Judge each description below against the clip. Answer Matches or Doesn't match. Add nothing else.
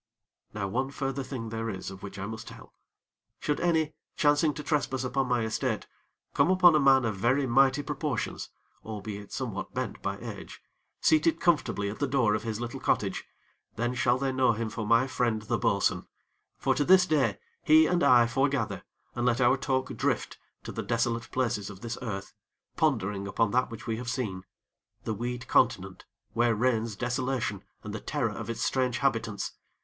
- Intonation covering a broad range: Doesn't match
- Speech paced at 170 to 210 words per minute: Matches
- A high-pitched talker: Doesn't match